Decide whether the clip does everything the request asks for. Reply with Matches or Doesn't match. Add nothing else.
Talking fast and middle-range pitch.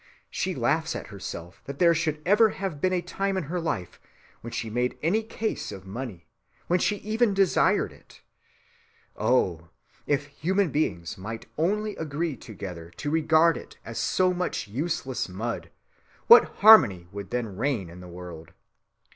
Doesn't match